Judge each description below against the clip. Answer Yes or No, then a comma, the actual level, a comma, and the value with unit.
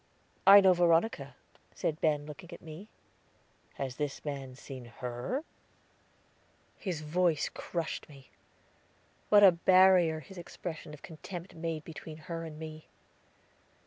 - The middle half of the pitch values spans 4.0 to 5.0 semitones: No, average, 3.1 semitones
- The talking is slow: Yes, slow, 125 wpm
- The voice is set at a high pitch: No, medium, 160 Hz